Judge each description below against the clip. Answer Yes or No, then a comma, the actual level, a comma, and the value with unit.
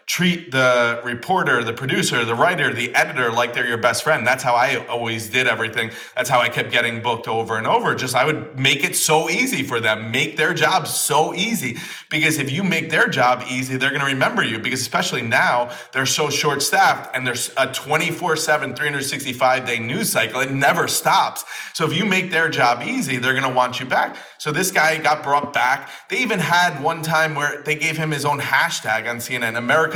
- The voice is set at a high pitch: No, low, 135 Hz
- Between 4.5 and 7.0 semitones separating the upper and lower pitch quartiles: No, average, 4.1 semitones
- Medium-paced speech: No, fast, 215 wpm